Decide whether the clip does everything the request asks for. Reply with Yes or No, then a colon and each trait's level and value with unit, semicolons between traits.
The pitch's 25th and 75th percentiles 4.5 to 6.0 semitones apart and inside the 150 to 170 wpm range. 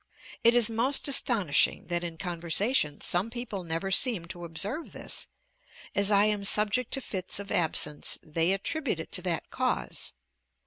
Yes: average, 5.2 semitones; average, 160 wpm